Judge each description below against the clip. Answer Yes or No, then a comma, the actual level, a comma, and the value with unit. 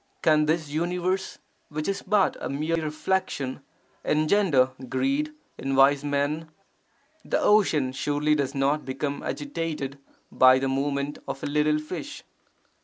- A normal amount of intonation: Yes, average, 3.4 semitones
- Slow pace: Yes, slow, 130 wpm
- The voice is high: No, medium, 150 Hz